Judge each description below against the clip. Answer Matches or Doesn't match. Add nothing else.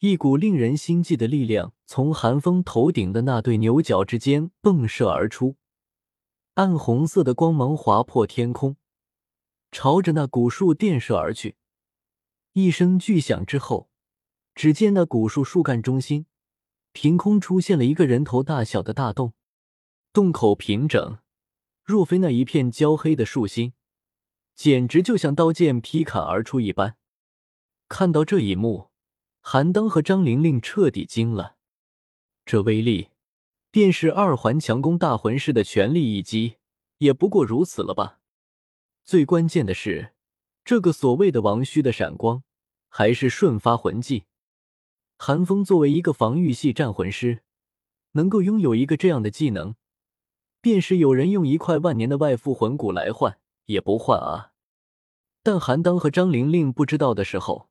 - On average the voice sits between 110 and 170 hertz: Matches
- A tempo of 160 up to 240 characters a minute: Matches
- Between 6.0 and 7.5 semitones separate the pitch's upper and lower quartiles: Matches